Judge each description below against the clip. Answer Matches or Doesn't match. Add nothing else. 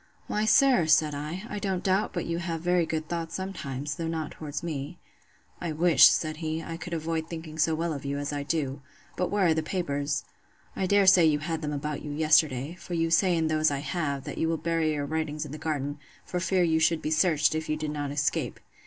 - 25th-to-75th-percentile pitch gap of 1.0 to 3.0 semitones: Matches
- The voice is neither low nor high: Matches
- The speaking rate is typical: Doesn't match